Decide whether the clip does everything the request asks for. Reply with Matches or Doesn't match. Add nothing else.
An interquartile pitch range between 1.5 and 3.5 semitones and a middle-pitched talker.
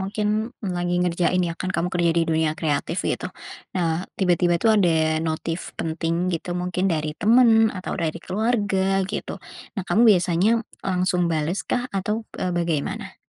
Matches